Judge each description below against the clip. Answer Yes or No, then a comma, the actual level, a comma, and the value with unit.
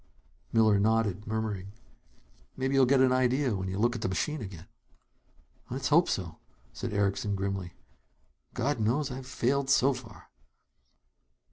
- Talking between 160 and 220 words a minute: No, average, 140 wpm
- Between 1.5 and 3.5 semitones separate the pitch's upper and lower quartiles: No, average, 4.8 semitones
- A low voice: Yes, low, 115 Hz